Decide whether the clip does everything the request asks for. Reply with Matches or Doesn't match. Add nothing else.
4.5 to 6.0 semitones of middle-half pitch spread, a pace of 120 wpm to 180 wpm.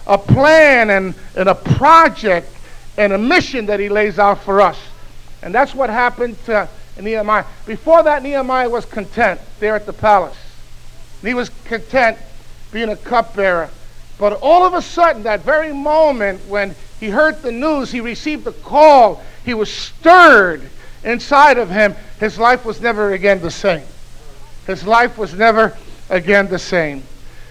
Matches